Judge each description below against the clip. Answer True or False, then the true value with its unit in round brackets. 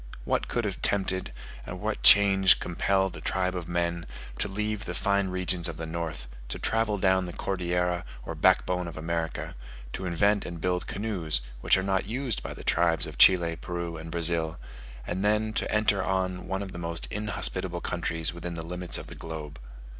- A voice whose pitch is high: False (90 Hz)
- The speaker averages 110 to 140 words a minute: False (190 wpm)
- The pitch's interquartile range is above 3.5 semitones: False (2.4 semitones)